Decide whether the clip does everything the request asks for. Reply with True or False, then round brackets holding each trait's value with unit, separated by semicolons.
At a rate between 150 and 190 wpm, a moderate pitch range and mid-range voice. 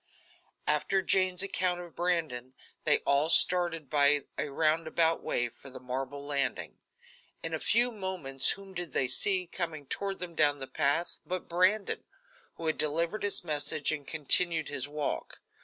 True (155 wpm; 4.0 semitones; 160 Hz)